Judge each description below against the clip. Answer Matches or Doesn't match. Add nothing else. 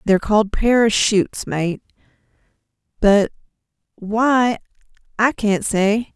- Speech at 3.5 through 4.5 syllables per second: Matches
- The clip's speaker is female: Matches